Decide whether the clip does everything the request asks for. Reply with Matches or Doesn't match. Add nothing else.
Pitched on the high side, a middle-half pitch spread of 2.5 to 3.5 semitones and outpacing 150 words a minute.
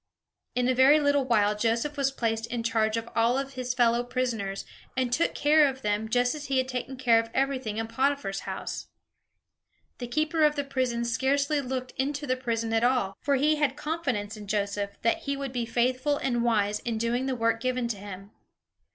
Matches